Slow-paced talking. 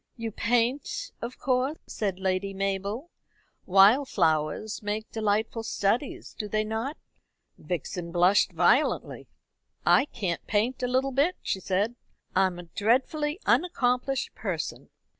Yes: slow, 125 wpm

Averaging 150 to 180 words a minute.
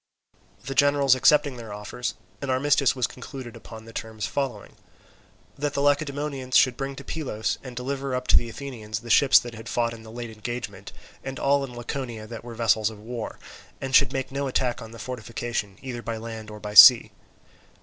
No: average, 195 wpm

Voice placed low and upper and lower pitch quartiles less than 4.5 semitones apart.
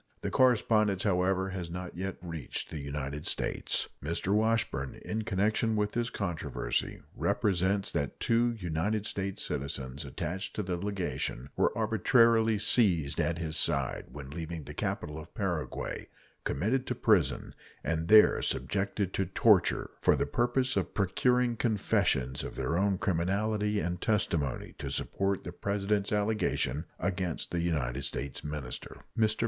No: very low, 95 Hz; average, 5.0 semitones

